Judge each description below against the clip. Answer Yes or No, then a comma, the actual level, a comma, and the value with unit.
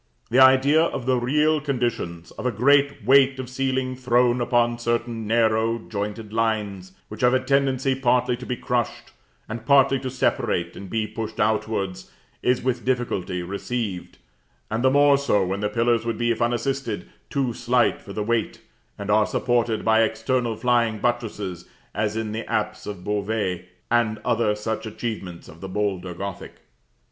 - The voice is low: Yes, low, 115 Hz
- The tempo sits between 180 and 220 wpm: No, average, 165 wpm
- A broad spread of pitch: No, average, 3.2 semitones